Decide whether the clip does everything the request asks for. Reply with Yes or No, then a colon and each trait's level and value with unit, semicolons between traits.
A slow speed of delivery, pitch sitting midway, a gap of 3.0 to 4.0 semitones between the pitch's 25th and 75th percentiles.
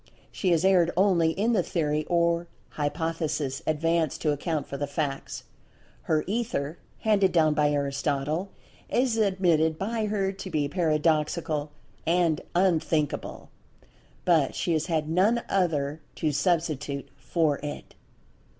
Yes: slow, 130 wpm; medium, 160 Hz; average, 3.5 semitones